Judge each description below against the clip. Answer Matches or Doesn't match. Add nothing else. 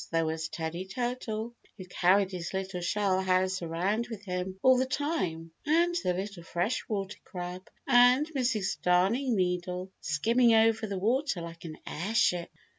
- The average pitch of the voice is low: Doesn't match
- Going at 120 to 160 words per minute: Matches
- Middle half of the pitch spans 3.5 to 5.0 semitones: Matches